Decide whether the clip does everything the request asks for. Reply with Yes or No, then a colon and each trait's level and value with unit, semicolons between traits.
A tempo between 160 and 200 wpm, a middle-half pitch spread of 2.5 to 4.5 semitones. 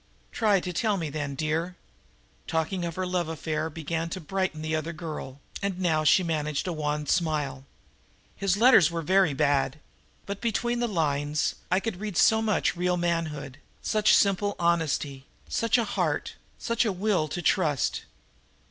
Yes: average, 165 wpm; average, 4.1 semitones